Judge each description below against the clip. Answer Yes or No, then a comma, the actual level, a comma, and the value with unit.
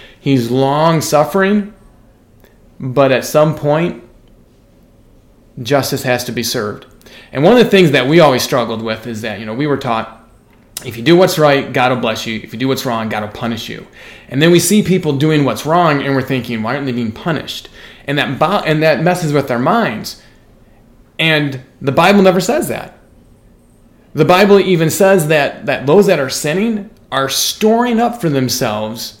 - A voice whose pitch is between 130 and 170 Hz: Yes, medium, 140 Hz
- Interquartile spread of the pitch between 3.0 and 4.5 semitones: No, wide, 5.5 semitones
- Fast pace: No, average, 190 wpm